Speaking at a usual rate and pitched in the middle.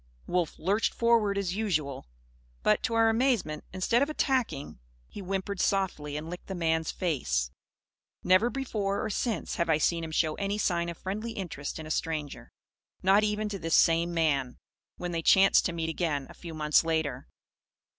Yes: average, 175 wpm; medium, 175 Hz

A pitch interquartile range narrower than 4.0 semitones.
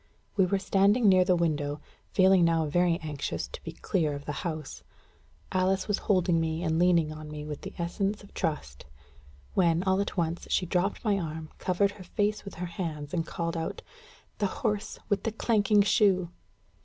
Yes: average, 3.5 semitones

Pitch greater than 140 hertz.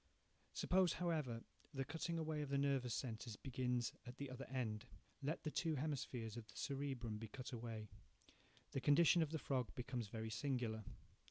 No: low, 130 Hz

